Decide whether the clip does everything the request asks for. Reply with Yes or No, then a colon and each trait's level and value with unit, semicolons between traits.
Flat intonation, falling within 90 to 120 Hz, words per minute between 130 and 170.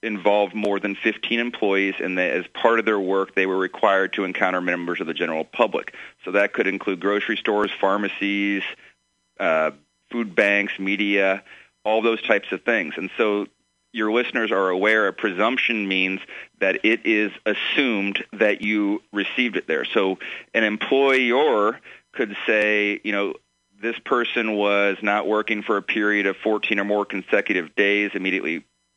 Yes: narrow, 1.8 semitones; low, 100 Hz; average, 160 wpm